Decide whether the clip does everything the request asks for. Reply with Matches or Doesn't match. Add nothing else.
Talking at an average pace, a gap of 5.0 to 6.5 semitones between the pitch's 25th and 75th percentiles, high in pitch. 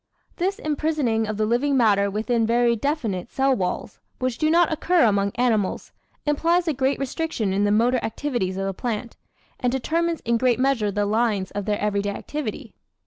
Matches